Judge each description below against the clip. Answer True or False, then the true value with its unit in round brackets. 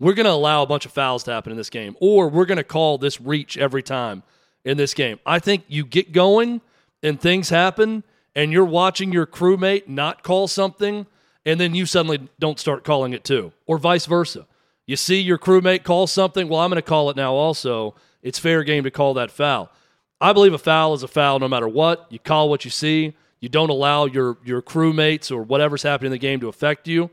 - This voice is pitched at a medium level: True (155 Hz)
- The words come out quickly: True (230 wpm)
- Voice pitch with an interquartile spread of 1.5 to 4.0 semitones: False (4.4 semitones)